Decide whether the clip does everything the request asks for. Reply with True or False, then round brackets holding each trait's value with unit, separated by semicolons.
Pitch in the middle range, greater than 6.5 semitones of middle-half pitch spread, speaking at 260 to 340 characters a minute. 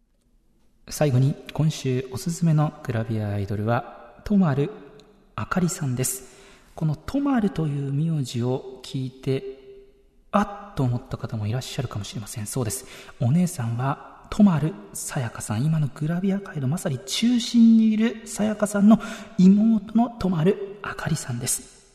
True (150 Hz; 7.6 semitones; 315 characters per minute)